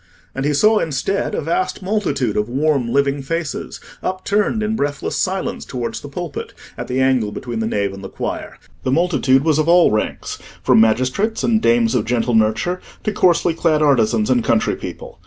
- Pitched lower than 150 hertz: Yes, medium, 140 Hz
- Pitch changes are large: Yes, wide, 7.0 semitones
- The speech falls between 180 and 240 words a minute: Yes, average, 185 wpm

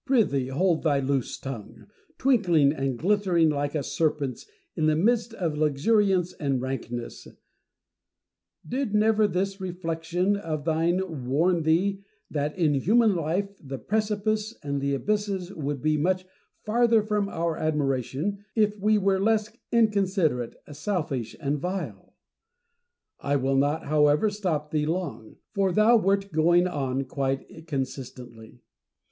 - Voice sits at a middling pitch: Yes, medium, 165 Hz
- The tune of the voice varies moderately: No, wide, 6.0 semitones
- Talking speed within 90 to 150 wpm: Yes, slow, 135 wpm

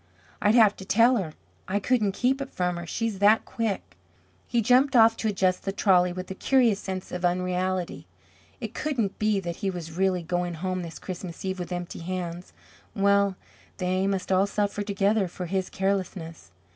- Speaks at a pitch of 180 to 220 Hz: Yes, high, 190 Hz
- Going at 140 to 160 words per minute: No, average, 185 wpm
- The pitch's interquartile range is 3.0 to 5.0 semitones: No, narrow, 2.5 semitones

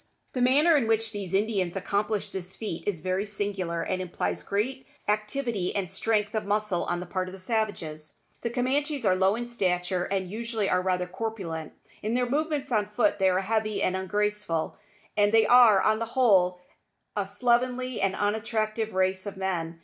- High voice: Yes, high, 205 Hz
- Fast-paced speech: No, average, 180 wpm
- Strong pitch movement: No, average, 3.4 semitones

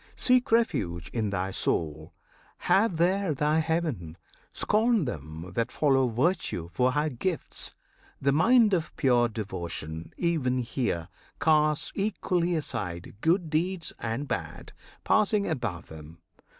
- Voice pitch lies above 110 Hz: Yes, medium, 140 Hz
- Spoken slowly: Yes, slow, 125 wpm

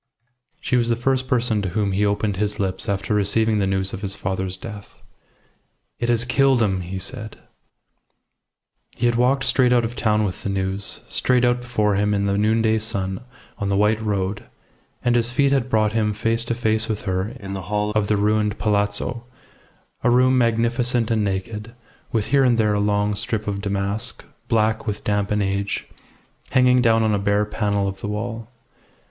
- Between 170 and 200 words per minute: Yes, average, 190 wpm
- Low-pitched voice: Yes, low, 105 Hz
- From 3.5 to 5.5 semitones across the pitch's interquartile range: No, narrow, 2.6 semitones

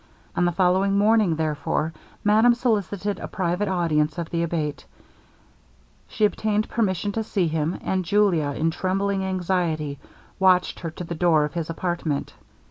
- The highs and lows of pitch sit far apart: No, average, 3.7 semitones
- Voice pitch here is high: No, medium, 180 Hz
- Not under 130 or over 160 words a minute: Yes, average, 150 wpm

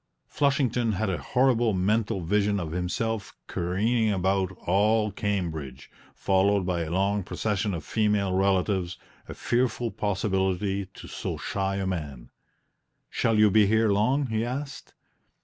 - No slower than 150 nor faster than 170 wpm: No, slow, 135 wpm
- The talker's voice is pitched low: Yes, low, 100 Hz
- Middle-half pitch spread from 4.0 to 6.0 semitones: No, average, 2.9 semitones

